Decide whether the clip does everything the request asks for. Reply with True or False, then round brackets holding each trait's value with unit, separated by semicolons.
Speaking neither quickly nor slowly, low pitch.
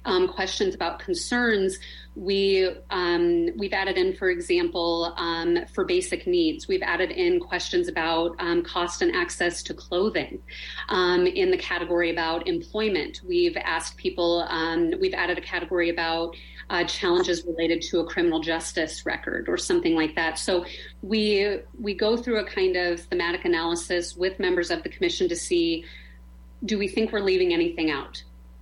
False (160 wpm; 185 Hz)